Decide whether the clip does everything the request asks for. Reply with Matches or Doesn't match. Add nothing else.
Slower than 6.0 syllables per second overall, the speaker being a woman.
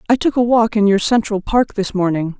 Matches